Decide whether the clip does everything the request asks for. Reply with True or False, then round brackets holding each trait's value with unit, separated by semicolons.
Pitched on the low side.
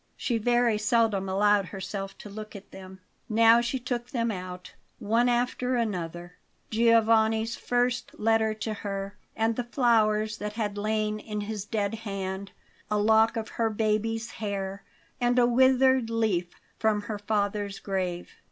False (215 Hz)